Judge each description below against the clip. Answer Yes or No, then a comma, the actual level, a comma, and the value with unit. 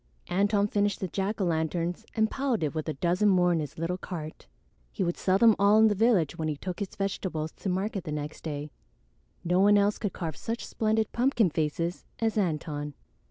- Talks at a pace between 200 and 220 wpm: Yes, fast, 205 wpm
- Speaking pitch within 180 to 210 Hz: Yes, medium, 185 Hz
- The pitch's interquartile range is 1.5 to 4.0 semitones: No, average, 4.4 semitones